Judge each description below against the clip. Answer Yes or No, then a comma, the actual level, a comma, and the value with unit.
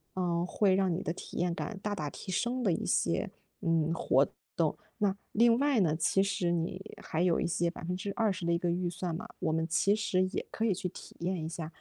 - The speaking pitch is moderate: Yes, medium, 180 Hz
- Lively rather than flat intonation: No, average, 2.8 semitones